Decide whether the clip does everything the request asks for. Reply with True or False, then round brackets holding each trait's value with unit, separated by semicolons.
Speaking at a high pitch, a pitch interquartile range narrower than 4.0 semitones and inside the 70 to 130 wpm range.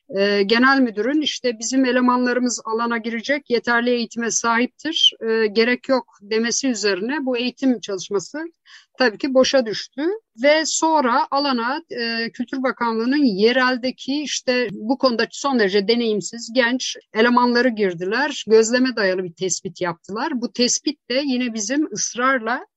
True (245 Hz; 3.1 semitones; 125 wpm)